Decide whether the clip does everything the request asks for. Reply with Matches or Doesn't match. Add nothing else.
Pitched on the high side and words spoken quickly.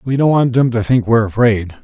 Doesn't match